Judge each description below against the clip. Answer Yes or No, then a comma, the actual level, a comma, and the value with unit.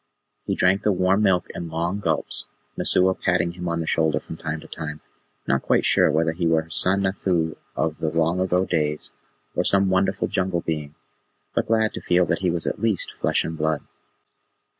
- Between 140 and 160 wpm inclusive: No, average, 200 wpm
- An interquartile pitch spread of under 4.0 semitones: Yes, narrow, 2.6 semitones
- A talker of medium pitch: No, very low, 85 Hz